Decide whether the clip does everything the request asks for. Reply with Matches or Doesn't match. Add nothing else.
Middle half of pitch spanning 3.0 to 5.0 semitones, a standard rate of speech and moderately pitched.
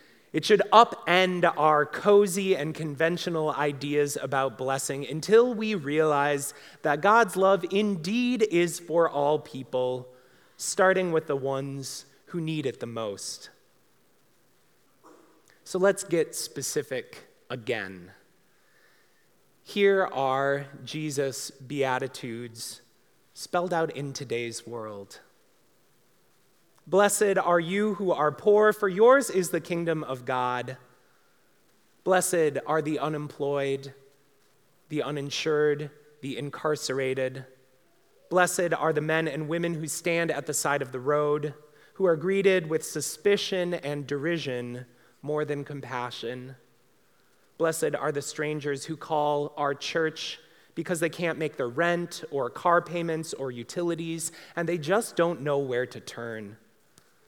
Doesn't match